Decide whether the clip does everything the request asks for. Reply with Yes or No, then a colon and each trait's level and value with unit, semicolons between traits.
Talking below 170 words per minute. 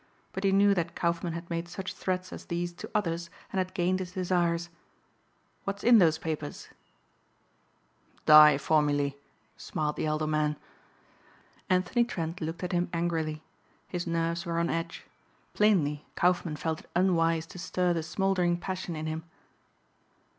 Yes: average, 150 wpm